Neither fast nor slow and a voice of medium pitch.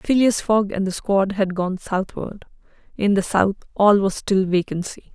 No: average, 175 wpm; high, 195 Hz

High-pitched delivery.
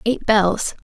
Yes: high, 215 Hz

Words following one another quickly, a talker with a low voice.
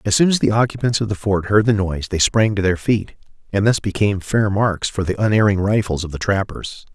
Yes: fast, 240 wpm; low, 100 Hz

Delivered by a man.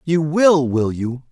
Yes: male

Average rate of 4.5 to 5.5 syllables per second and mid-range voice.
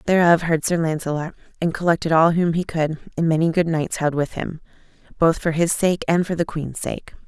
Yes: 5.3 syllables/s; medium, 165 Hz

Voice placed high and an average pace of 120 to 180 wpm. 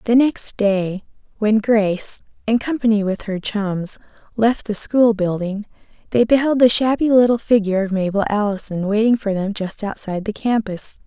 Yes: high, 215 Hz; average, 165 wpm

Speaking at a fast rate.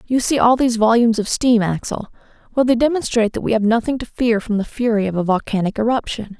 Yes: fast, 225 wpm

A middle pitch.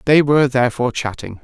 No: low, 130 Hz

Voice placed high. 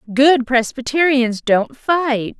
Yes: very high, 255 Hz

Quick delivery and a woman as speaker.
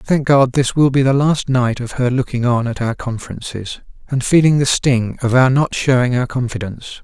No: fast, 215 wpm; male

